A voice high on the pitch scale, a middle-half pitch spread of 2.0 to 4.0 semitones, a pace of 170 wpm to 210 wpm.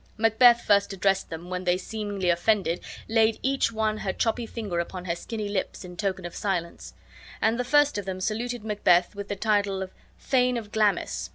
Yes: high, 205 Hz; average, 3.2 semitones; average, 190 wpm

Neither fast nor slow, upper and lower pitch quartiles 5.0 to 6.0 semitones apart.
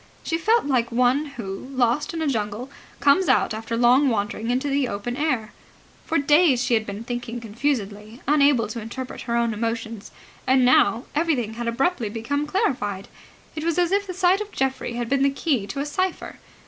No: average, 190 wpm; average, 4.3 semitones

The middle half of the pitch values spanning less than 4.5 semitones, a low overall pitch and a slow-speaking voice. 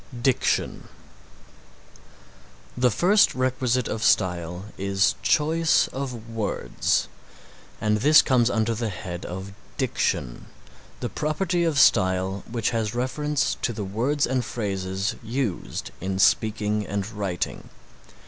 No: average, 4.9 semitones; low, 110 Hz; slow, 115 wpm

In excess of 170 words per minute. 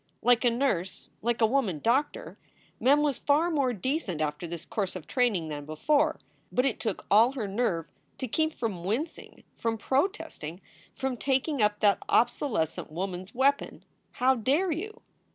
No: average, 165 wpm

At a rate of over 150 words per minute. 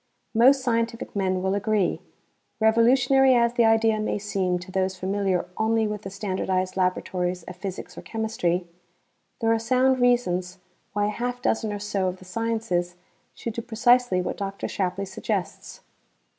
Yes: average, 160 wpm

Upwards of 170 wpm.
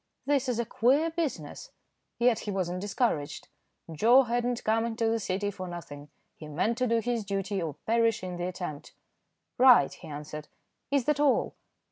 Yes: average, 180 wpm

